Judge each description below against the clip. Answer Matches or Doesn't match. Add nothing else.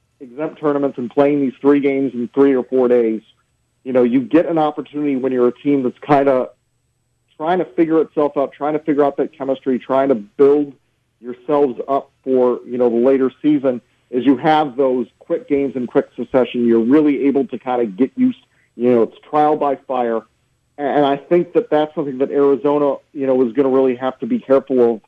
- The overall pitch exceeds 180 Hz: Doesn't match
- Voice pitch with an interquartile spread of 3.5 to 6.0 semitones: Doesn't match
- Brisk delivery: Matches